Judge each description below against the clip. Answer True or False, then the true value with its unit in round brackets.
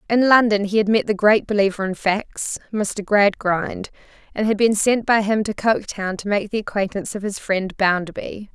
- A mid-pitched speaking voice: False (205 Hz)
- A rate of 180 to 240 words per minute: True (195 wpm)